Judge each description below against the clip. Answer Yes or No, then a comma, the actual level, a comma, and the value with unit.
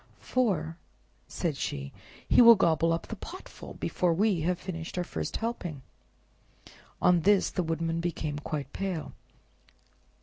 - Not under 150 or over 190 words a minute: No, slow, 135 wpm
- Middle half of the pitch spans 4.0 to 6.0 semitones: No, average, 3.2 semitones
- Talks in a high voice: No, medium, 170 Hz